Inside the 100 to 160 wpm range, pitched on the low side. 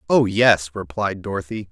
Yes: average, 140 wpm; low, 100 Hz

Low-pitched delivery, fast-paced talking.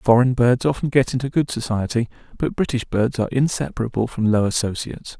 No: low, 120 Hz; average, 175 wpm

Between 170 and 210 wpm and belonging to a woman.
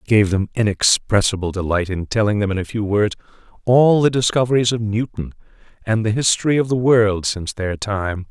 No: average, 190 wpm; male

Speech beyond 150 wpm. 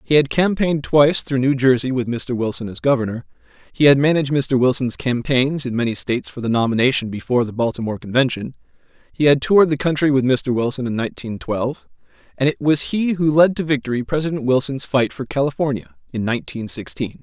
Yes: average, 190 wpm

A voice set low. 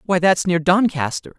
No: medium, 175 Hz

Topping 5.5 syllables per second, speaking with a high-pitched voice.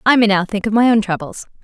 Yes: 6.5 syllables/s; high, 210 Hz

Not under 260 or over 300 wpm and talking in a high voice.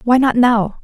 No: fast, 215 wpm; high, 235 Hz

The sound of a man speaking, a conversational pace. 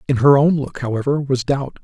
No: male; fast, 230 wpm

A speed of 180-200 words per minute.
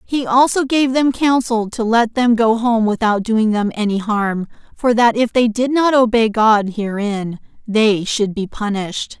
Yes: average, 185 wpm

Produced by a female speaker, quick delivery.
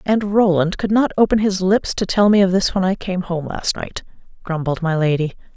Yes: female; fast, 225 wpm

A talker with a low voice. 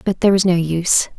No: medium, 180 Hz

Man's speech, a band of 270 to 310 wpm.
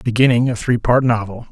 No: male; average, 200 wpm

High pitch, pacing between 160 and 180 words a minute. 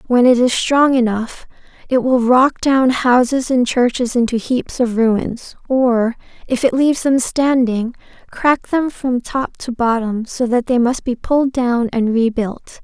Yes: high, 245 Hz; average, 175 wpm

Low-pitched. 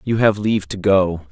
Yes: low, 100 Hz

